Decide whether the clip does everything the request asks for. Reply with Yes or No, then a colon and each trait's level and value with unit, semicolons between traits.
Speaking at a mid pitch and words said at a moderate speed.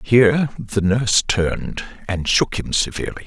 No: low, 110 Hz; average, 145 wpm